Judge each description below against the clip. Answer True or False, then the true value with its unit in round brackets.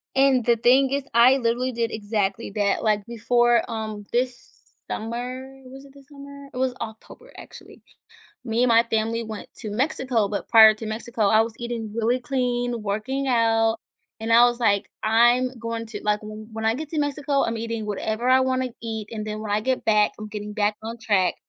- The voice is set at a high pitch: True (230 Hz)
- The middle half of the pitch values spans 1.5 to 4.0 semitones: True (2.8 semitones)